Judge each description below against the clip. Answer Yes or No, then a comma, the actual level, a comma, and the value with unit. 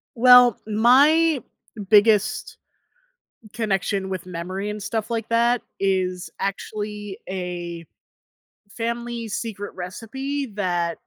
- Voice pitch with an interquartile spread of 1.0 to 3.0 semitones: No, average, 3.8 semitones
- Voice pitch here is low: No, high, 210 Hz